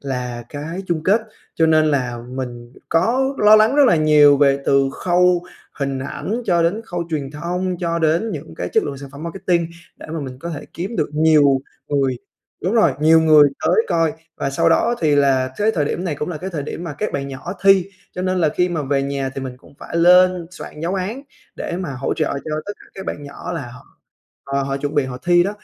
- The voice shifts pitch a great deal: No, average, 4.4 semitones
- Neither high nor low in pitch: Yes, medium, 160 Hz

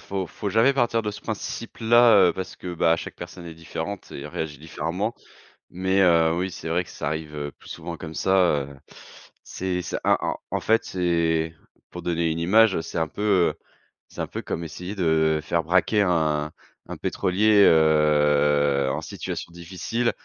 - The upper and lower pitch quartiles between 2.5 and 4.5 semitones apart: Yes, average, 3.4 semitones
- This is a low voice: Yes, very low, 85 Hz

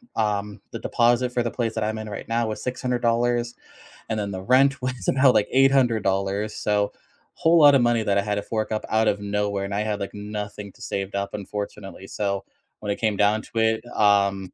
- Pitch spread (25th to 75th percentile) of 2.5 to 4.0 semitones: Yes, average, 2.8 semitones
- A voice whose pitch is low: Yes, low, 105 Hz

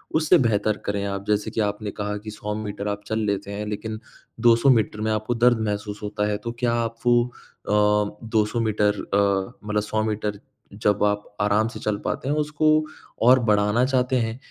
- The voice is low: Yes, low, 105 Hz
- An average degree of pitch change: No, narrow, 2.1 semitones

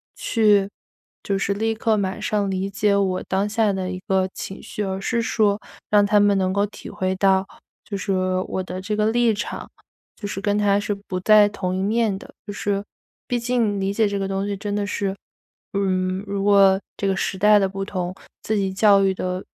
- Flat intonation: Yes, narrow, 1.4 semitones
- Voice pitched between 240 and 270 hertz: No, high, 200 Hz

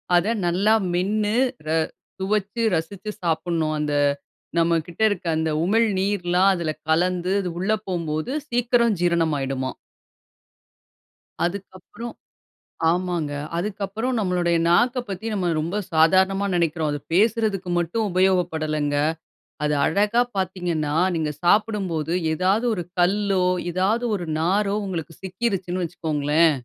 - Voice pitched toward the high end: No, medium, 180 Hz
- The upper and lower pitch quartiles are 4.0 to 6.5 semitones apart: No, average, 3.6 semitones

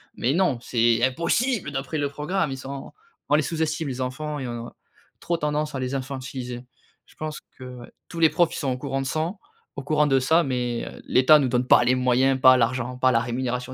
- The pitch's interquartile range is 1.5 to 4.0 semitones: Yes, average, 3.1 semitones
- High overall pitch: No, low, 135 Hz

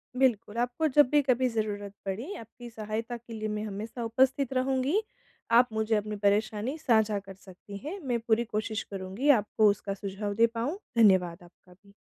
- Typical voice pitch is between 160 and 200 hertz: No, high, 220 Hz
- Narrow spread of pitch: No, average, 3.5 semitones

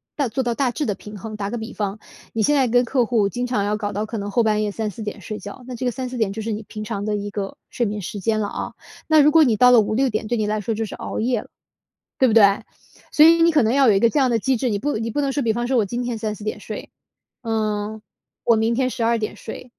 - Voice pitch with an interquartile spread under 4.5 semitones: Yes, average, 2.8 semitones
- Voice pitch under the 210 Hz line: No, high, 225 Hz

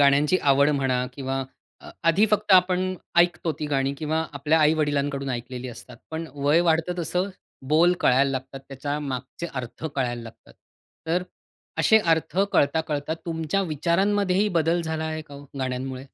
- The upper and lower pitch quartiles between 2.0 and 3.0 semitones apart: No, average, 3.7 semitones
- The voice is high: No, medium, 150 Hz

